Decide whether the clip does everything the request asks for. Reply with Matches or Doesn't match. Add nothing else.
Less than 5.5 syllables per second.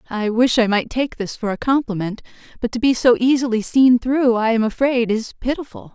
Matches